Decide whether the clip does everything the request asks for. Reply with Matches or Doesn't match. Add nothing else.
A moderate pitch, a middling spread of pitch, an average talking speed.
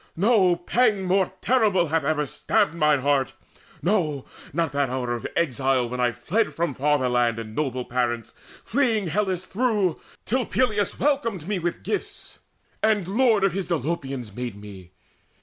Doesn't match